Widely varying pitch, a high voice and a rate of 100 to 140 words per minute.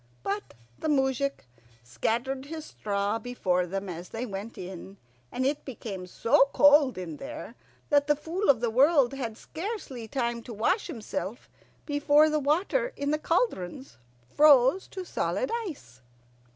No: wide, 6.1 semitones; very high, 265 Hz; average, 150 wpm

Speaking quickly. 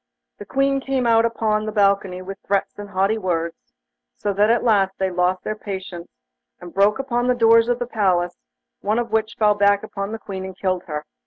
Yes: fast, 210 wpm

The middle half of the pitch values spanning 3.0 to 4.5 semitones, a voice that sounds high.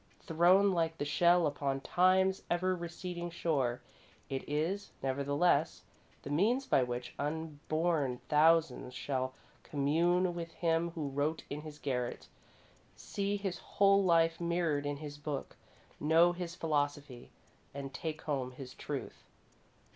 No: average, 3.4 semitones; medium, 160 Hz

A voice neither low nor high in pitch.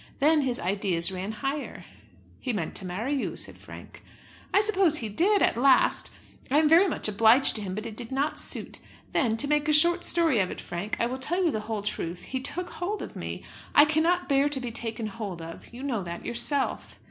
No: very high, 255 Hz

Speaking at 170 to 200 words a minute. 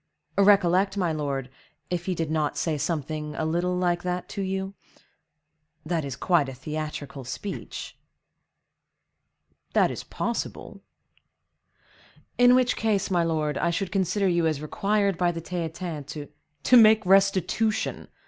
No: slow, 135 wpm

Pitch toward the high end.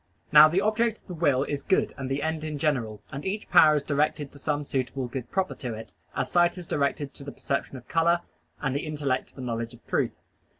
No: medium, 145 Hz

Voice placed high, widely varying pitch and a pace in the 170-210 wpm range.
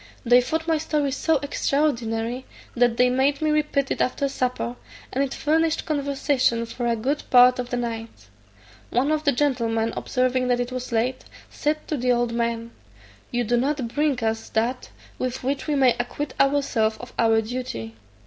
No: very high, 250 Hz; average, 3.2 semitones; average, 175 wpm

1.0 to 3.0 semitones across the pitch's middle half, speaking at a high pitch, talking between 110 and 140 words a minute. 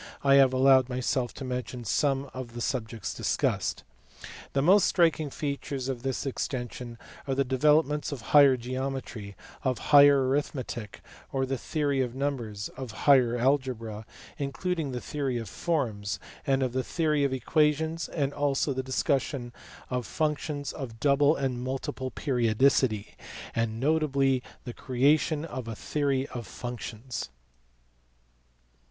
No: average, 2.7 semitones; low, 135 Hz; slow, 135 wpm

